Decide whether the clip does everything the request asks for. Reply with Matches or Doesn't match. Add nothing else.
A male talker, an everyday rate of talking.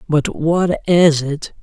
Matches